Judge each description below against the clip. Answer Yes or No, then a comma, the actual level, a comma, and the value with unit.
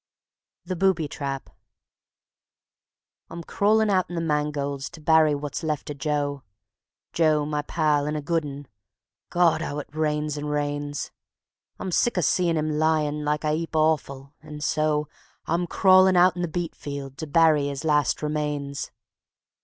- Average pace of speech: Yes, average, 160 wpm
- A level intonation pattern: Yes, narrow, 2.1 semitones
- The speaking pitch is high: No, medium, 150 Hz